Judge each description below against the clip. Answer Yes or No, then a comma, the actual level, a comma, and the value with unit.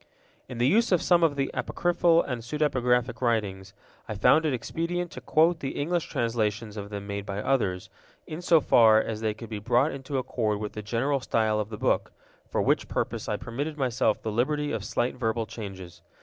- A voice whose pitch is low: Yes, low, 120 Hz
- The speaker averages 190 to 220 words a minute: Yes, average, 200 wpm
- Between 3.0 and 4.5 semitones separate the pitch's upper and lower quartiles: No, wide, 5.5 semitones